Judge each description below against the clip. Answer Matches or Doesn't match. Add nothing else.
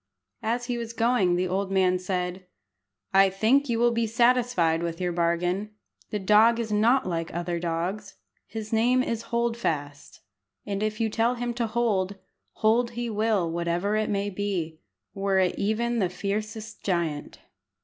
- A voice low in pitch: Doesn't match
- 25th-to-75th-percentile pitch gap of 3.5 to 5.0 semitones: Matches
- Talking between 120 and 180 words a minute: Matches